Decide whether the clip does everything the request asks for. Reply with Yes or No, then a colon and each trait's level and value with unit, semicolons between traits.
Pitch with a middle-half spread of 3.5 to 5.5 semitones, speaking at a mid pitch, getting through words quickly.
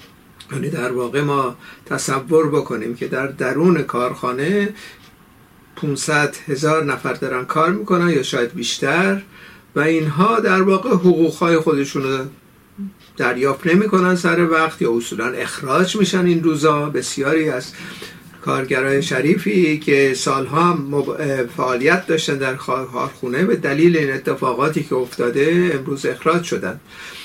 No: average, 4.6 semitones; medium, 155 Hz; average, 125 wpm